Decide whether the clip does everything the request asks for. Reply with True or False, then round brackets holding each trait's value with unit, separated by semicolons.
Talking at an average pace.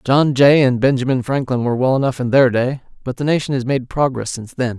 False (240 wpm)